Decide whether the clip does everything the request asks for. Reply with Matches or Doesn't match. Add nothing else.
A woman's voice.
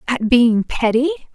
Matches